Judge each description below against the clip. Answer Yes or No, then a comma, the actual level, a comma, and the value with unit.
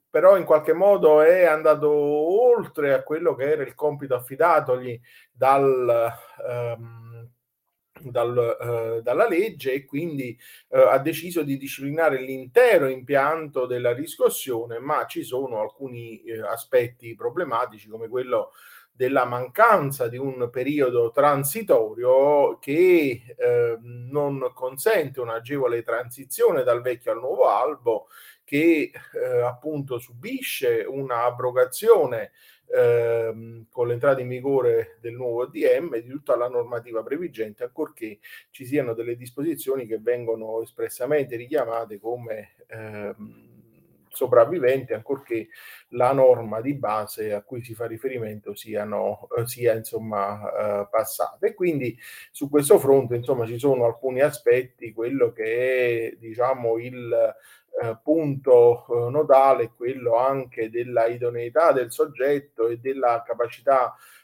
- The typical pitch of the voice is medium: No, low, 130 Hz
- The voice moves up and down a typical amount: No, wide, 5.8 semitones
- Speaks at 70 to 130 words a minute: Yes, average, 120 wpm